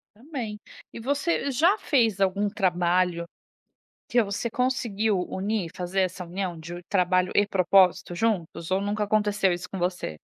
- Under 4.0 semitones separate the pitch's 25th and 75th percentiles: Yes, average, 3.6 semitones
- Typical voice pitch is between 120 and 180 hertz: No, high, 195 Hz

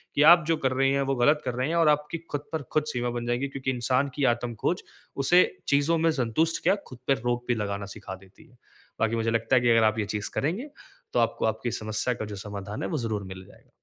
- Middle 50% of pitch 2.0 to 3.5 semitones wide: No, average, 4.4 semitones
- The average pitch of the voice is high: No, low, 125 Hz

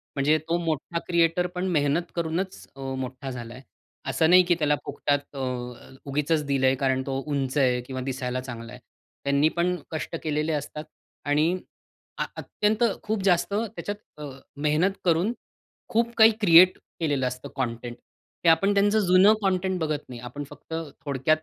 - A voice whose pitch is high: No, medium, 150 Hz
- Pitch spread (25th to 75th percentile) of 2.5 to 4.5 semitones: No, average, 4.9 semitones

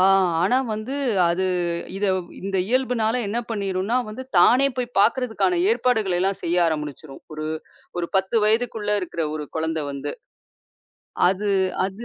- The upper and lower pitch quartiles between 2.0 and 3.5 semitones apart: No, average, 5.3 semitones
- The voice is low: No, high, 200 Hz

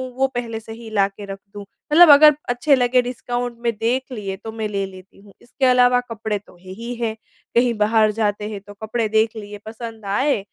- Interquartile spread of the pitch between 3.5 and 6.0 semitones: No, average, 2.9 semitones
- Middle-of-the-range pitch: No, high, 225 Hz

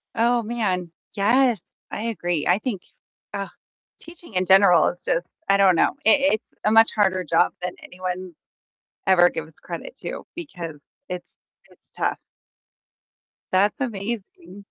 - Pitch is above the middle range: Yes, high, 195 Hz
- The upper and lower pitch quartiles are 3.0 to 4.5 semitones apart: Yes, average, 4.1 semitones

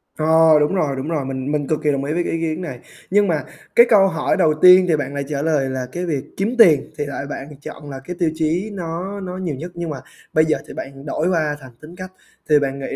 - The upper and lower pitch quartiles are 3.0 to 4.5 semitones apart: Yes, average, 3.8 semitones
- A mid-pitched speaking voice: Yes, medium, 155 Hz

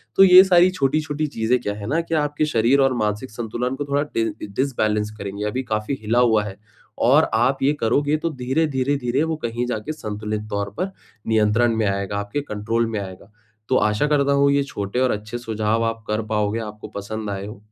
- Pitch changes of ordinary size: Yes, average, 4.8 semitones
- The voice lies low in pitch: Yes, low, 115 Hz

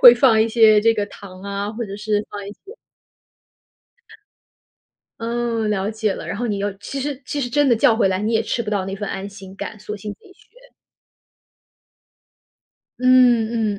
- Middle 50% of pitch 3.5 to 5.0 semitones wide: No, average, 2.8 semitones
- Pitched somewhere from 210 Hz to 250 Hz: Yes, high, 215 Hz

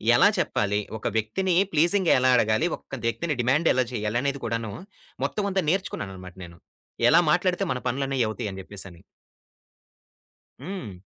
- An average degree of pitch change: No, wide, 8.0 semitones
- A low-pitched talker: Yes, low, 125 Hz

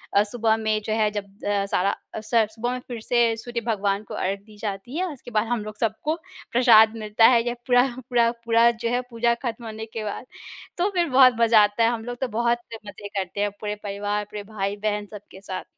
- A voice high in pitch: Yes, high, 220 Hz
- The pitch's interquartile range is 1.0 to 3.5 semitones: Yes, narrow, 2.4 semitones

